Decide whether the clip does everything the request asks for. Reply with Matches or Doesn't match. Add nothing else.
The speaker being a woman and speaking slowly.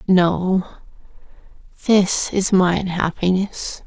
Matches